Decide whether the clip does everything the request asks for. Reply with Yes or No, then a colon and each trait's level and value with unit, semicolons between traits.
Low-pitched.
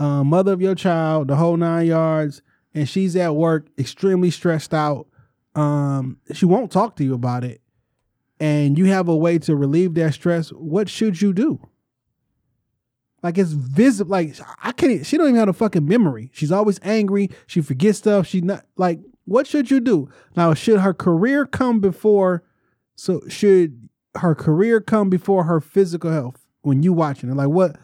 No: medium, 170 Hz